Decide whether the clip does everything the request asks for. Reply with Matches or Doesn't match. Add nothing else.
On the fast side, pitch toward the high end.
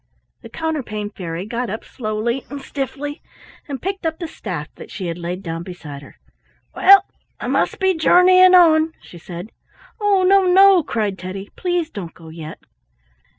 Doesn't match